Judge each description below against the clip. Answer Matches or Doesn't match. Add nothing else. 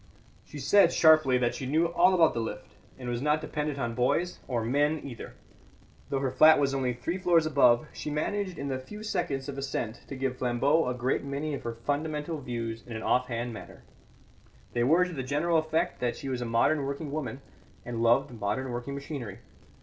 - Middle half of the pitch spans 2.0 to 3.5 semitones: Doesn't match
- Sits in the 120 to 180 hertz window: Matches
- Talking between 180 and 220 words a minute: Matches